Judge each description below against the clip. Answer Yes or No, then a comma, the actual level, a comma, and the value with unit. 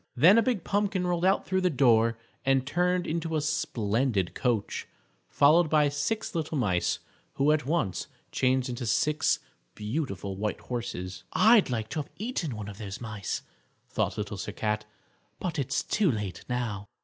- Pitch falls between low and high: No, low, 130 Hz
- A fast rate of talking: No, average, 165 wpm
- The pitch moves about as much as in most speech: No, wide, 7.5 semitones